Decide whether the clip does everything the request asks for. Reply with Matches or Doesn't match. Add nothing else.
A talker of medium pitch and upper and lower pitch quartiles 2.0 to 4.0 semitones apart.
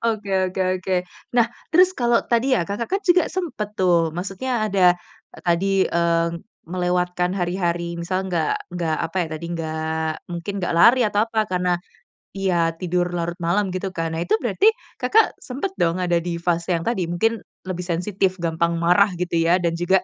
Matches